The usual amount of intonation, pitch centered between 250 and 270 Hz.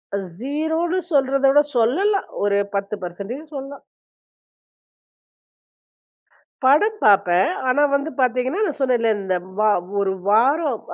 No: wide, 5.8 semitones; very high, 265 Hz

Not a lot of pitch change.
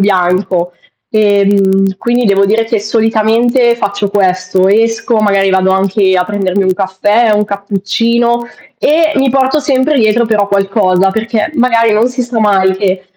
No: average, 3.3 semitones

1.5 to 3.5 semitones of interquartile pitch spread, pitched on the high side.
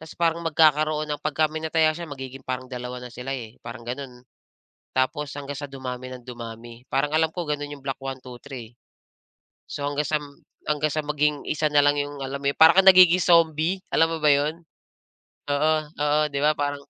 No: average, 2.8 semitones; medium, 145 Hz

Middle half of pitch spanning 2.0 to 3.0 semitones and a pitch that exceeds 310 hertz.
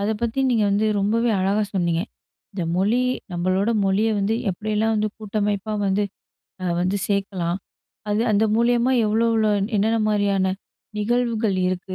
No: narrow, 2.5 semitones; high, 210 Hz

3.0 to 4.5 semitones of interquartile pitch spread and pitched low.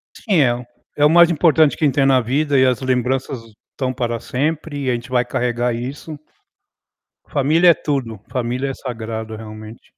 Yes: average, 3.3 semitones; low, 130 Hz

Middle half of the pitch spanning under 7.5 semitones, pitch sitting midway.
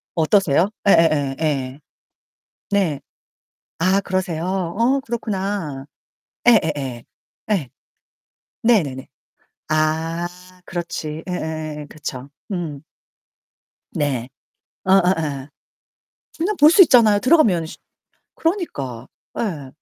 Yes: wide, 5.4 semitones; medium, 165 Hz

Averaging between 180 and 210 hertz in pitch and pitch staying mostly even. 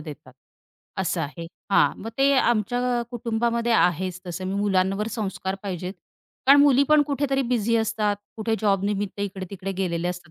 No: high, 205 Hz; average, 4.0 semitones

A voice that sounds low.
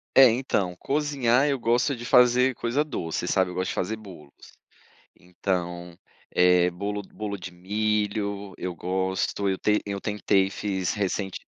Yes: low, 100 Hz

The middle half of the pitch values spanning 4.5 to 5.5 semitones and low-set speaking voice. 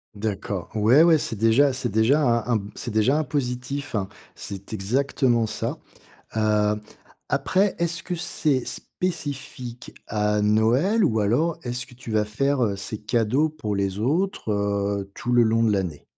Yes: average, 5.0 semitones; low, 120 Hz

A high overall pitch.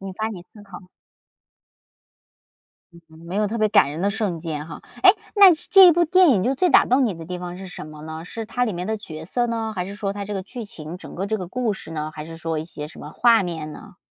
Yes: high, 195 Hz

